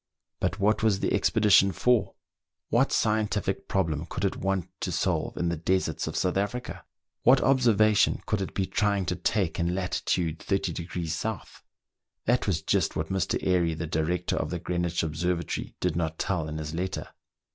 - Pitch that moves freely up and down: No, average, 3.5 semitones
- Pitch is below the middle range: Yes, very low, 90 Hz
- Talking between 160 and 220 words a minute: Yes, average, 170 wpm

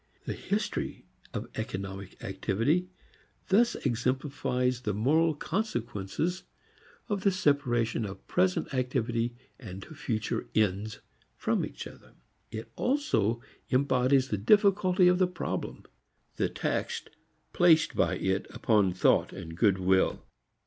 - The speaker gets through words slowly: Yes, slow, 115 wpm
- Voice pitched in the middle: No, low, 125 Hz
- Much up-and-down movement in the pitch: Yes, wide, 8.1 semitones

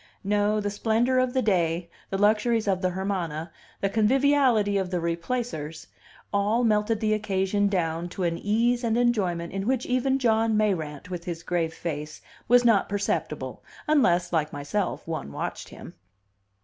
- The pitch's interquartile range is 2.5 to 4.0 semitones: No, average, 4.7 semitones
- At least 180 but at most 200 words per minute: No, average, 160 wpm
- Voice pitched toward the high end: Yes, high, 205 Hz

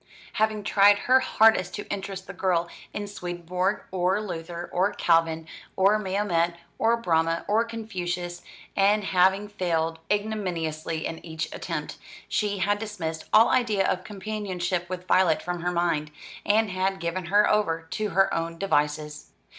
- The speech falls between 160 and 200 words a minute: No, average, 145 wpm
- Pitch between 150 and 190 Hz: Yes, medium, 185 Hz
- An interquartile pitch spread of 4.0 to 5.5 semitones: No, average, 3.5 semitones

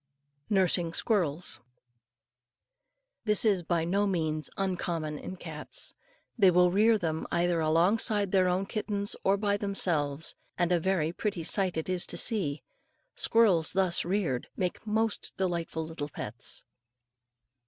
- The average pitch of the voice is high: No, medium, 180 Hz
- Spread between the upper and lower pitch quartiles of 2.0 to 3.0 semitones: No, average, 3.6 semitones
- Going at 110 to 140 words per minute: Yes, slow, 135 wpm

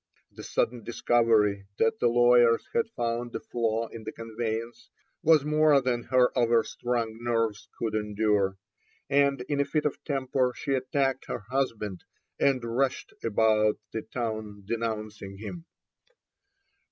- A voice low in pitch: Yes, low, 115 Hz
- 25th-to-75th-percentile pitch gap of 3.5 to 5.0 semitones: No, average, 2.9 semitones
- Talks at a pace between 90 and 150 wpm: Yes, slow, 135 wpm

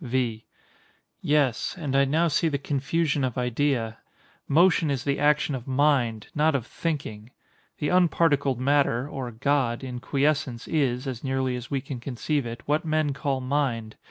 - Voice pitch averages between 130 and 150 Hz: Yes, medium, 140 Hz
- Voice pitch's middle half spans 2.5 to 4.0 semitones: Yes, average, 3.1 semitones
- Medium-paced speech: Yes, average, 160 wpm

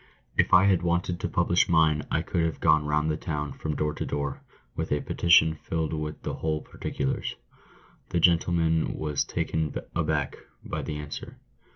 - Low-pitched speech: Yes, very low, 80 Hz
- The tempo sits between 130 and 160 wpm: No, average, 175 wpm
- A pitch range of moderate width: No, narrow, 1.9 semitones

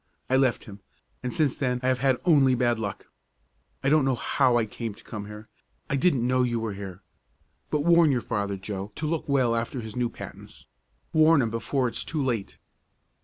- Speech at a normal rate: No, fast, 210 wpm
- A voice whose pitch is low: Yes, low, 125 Hz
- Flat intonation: No, average, 3.7 semitones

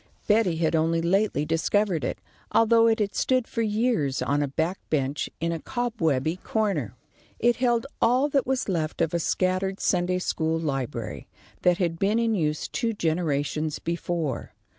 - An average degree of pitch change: No, wide, 5.7 semitones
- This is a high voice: No, medium, 175 Hz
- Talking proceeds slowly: No, average, 160 wpm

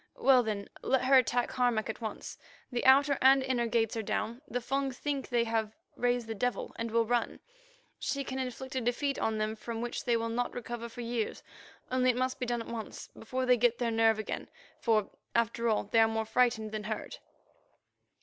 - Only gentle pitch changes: Yes, narrow, 2.2 semitones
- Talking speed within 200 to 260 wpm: Yes, fast, 205 wpm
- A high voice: Yes, high, 235 Hz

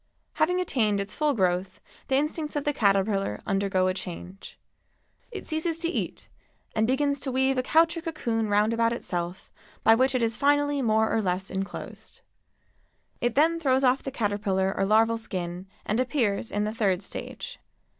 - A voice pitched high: Yes, high, 225 Hz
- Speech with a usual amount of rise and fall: No, wide, 6.2 semitones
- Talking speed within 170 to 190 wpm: Yes, average, 175 wpm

